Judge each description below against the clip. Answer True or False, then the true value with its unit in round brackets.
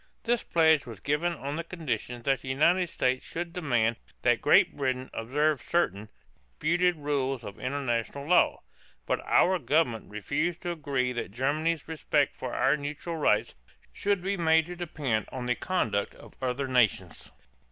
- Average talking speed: True (160 wpm)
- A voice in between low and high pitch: True (145 Hz)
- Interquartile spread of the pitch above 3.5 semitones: True (5.0 semitones)